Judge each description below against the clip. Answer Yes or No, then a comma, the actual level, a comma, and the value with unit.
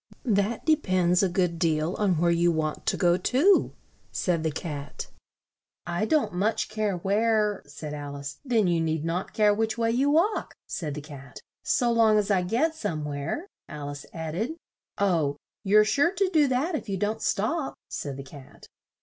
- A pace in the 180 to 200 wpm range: Yes, average, 190 wpm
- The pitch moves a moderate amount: No, wide, 6.2 semitones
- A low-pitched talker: No, high, 190 Hz